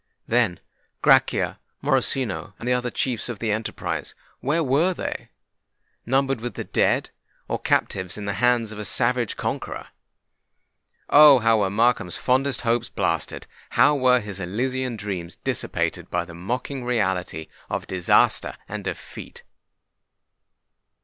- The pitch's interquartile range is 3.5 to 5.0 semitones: Yes, average, 4.4 semitones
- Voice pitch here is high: No, low, 115 Hz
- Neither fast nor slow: No, slow, 125 wpm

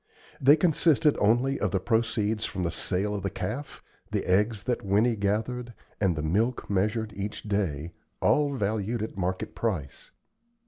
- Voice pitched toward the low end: Yes, low, 105 Hz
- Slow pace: No, average, 165 wpm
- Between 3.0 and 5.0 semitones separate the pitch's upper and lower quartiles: Yes, average, 3.5 semitones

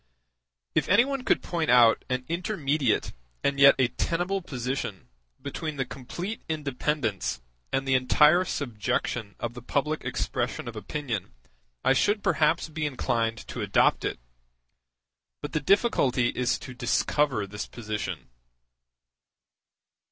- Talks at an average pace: No, slow, 130 wpm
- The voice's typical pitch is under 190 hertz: Yes, medium, 140 Hz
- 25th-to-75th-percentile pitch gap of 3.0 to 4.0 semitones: No, average, 4.4 semitones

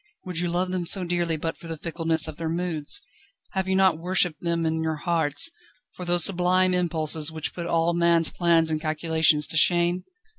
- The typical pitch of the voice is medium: Yes, medium, 170 Hz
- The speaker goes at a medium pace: Yes, average, 195 wpm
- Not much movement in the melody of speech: Yes, narrow, 1.8 semitones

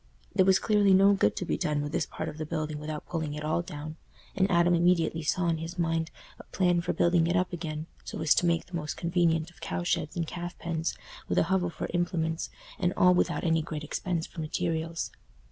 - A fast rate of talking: Yes, fast, 230 wpm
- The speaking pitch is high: No, medium, 165 Hz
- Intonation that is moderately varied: No, narrow, 1.9 semitones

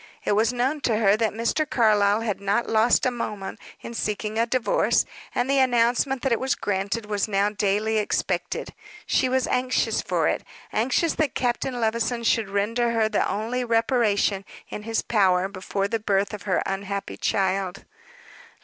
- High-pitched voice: Yes, high, 220 Hz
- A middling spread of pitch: Yes, average, 3.1 semitones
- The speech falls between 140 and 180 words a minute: Yes, average, 170 wpm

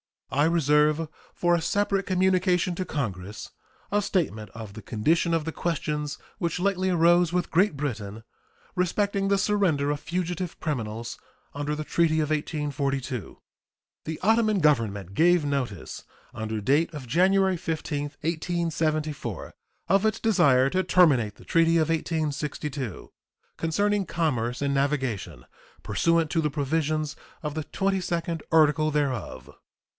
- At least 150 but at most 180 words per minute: No, slow, 135 wpm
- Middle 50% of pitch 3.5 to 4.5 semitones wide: Yes, average, 4.0 semitones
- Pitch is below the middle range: No, medium, 155 Hz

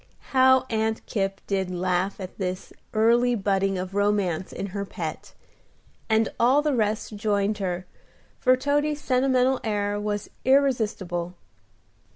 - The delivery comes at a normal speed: No, slow, 130 wpm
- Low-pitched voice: No, high, 210 Hz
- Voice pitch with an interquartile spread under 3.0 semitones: No, average, 4.3 semitones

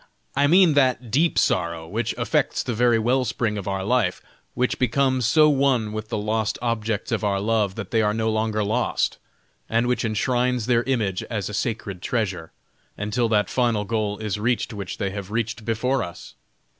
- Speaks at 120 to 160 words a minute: No, average, 185 wpm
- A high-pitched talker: No, low, 110 Hz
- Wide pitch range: No, average, 2.9 semitones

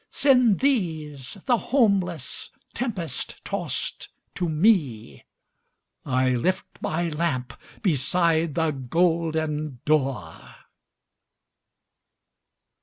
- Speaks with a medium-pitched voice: Yes, medium, 160 Hz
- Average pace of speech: No, slow, 75 wpm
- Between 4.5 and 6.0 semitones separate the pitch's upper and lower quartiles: Yes, average, 5.1 semitones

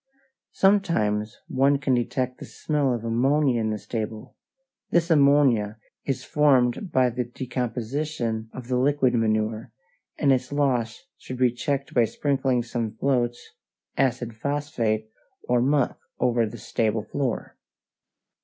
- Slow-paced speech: Yes, slow, 130 wpm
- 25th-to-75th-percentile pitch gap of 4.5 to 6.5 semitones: No, average, 3.5 semitones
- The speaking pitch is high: No, low, 125 Hz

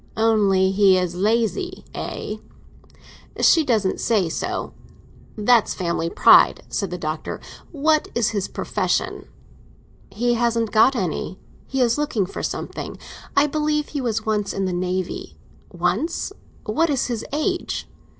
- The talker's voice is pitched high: Yes, high, 220 Hz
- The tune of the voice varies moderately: No, wide, 6.0 semitones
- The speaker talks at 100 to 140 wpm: Yes, slow, 135 wpm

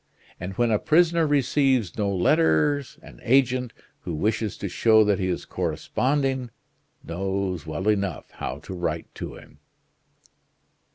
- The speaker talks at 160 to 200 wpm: No, slow, 135 wpm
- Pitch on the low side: Yes, low, 105 Hz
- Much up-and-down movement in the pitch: Yes, wide, 6.0 semitones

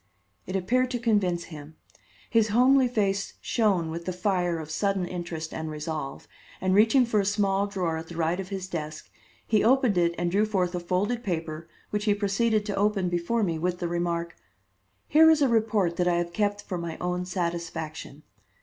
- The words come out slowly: No, average, 195 wpm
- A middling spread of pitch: Yes, average, 3.6 semitones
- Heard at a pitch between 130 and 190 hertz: Yes, medium, 185 Hz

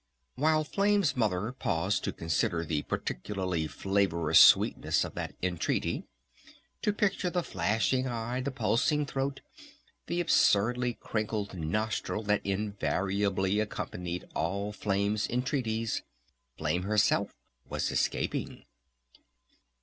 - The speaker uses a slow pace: Yes, slow, 105 wpm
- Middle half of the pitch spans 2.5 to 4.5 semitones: No, average, 5.0 semitones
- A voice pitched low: Yes, low, 105 Hz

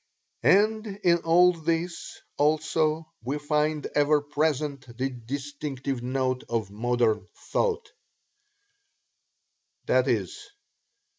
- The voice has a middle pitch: Yes, medium, 150 Hz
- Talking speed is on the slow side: Yes, slow, 85 wpm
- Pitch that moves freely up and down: No, average, 4.2 semitones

